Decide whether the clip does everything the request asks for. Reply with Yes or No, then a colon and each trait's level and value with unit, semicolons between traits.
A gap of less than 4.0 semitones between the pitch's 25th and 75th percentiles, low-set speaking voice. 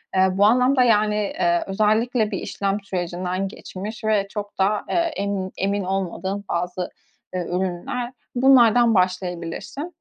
No: average, 2.9 semitones; high, 200 Hz